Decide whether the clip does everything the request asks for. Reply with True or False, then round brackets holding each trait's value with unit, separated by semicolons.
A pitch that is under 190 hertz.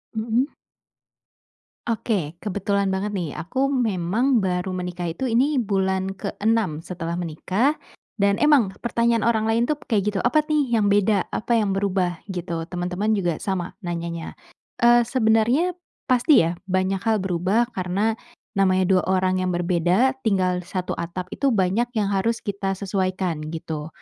False (195 Hz)